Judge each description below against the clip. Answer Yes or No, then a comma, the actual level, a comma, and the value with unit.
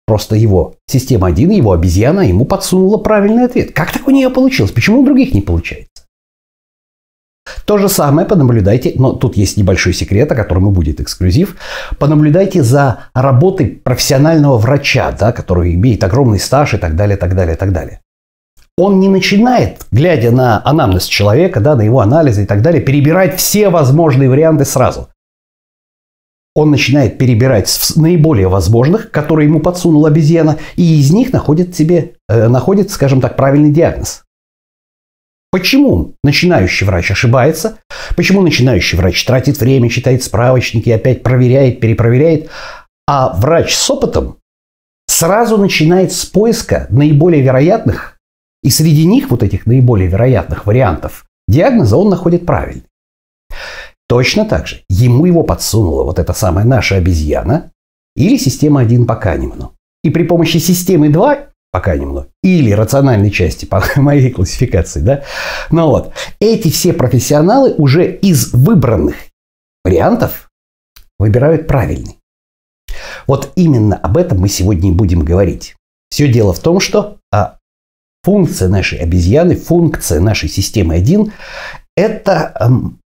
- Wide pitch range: Yes, wide, 9.0 semitones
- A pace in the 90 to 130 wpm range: No, average, 140 wpm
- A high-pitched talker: No, low, 130 Hz